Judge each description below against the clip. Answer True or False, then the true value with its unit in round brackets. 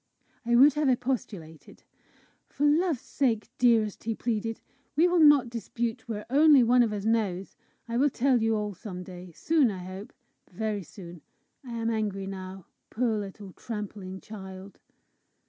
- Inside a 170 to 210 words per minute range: False (155 wpm)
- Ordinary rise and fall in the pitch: True (4.1 semitones)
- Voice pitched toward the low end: False (220 Hz)